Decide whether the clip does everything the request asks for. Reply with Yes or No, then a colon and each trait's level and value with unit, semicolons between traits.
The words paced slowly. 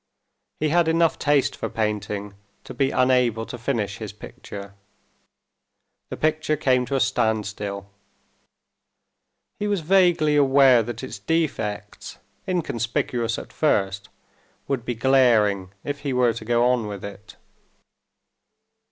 Yes: slow, 125 wpm